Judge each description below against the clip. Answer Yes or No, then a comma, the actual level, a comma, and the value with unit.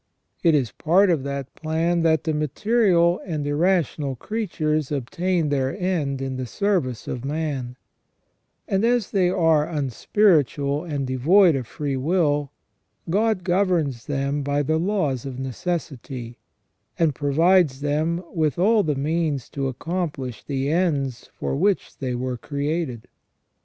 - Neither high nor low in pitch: Yes, medium, 150 Hz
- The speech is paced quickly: No, slow, 135 wpm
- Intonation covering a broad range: No, average, 4.4 semitones